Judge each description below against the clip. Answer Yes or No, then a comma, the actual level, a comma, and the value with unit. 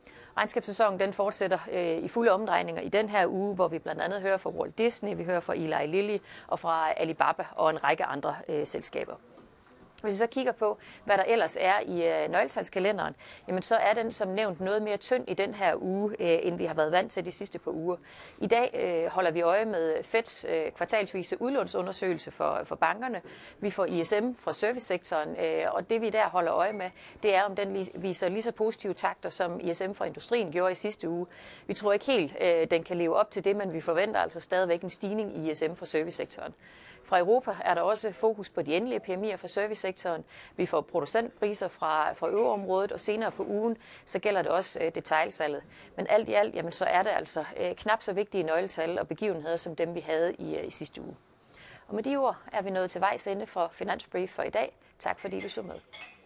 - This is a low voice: No, high, 200 Hz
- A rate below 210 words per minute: No, average, 215 wpm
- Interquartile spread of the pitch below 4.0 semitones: Yes, average, 3.6 semitones